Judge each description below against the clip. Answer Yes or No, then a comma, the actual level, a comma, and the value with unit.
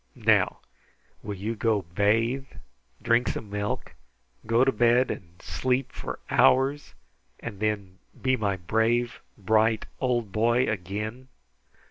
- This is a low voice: Yes, low, 110 Hz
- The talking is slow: Yes, slow, 120 wpm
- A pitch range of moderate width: Yes, average, 3.1 semitones